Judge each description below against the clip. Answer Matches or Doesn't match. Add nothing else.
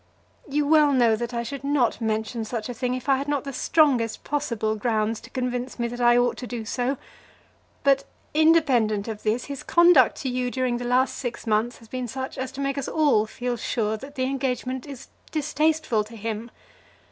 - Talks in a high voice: Matches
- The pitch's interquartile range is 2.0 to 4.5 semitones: Matches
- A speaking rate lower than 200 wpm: Doesn't match